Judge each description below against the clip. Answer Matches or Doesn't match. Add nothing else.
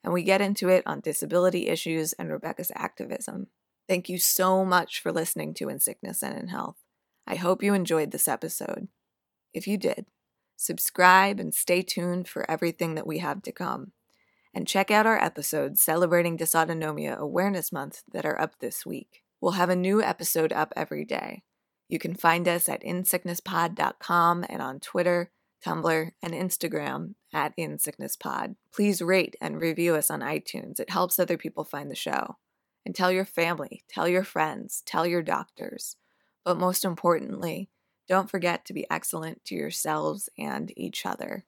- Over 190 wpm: Doesn't match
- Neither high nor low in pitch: Matches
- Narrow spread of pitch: Matches